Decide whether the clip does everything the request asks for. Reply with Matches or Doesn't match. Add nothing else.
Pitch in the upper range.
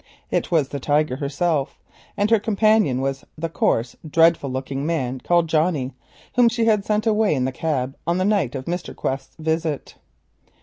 Doesn't match